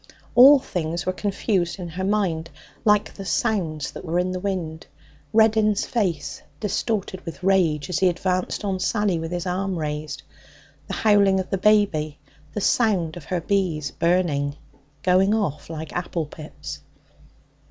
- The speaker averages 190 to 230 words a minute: No, average, 155 wpm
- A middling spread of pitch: Yes, average, 3.7 semitones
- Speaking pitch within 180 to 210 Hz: Yes, medium, 185 Hz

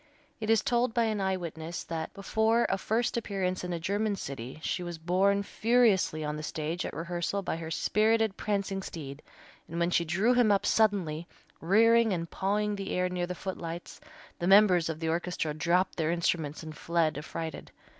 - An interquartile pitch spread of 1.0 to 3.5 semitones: No, average, 3.9 semitones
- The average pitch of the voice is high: No, medium, 180 Hz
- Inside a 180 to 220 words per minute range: Yes, average, 185 wpm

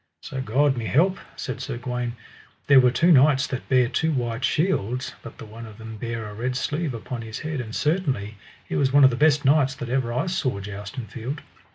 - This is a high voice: No, low, 125 Hz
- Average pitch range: Yes, average, 3.7 semitones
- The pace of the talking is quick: Yes, fast, 225 wpm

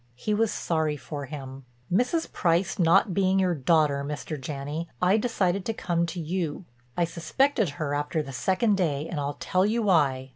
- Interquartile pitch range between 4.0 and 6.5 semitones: Yes, average, 4.7 semitones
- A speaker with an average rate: Yes, average, 180 wpm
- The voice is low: No, medium, 170 Hz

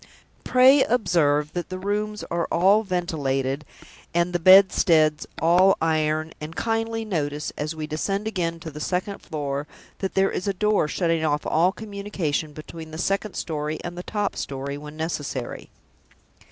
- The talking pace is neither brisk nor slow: Yes, average, 155 wpm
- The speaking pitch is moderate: Yes, medium, 170 Hz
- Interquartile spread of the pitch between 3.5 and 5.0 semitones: Yes, average, 4.4 semitones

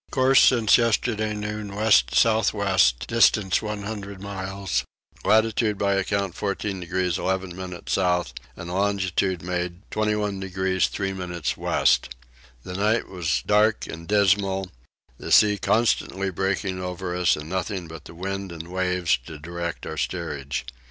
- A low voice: Yes, very low, 95 Hz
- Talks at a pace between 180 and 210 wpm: No, average, 140 wpm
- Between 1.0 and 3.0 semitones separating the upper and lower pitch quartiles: Yes, average, 2.7 semitones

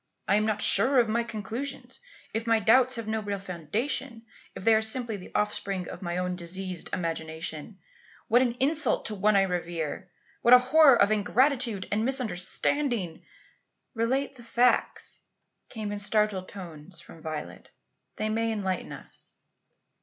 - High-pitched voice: Yes, high, 215 Hz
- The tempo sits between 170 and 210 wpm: No, average, 160 wpm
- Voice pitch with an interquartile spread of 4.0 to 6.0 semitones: Yes, average, 4.3 semitones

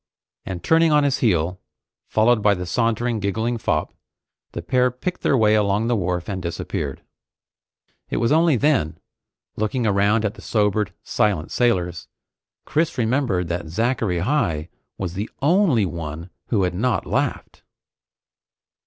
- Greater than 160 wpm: No, average, 145 wpm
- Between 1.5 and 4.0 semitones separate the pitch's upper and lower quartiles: No, wide, 5.4 semitones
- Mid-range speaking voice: No, low, 105 Hz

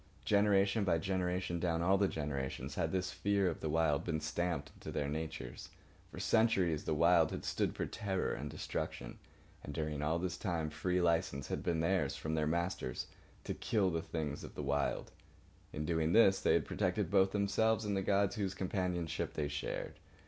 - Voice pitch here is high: No, very low, 85 Hz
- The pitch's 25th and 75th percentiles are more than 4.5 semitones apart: No, average, 3.7 semitones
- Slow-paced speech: No, average, 185 wpm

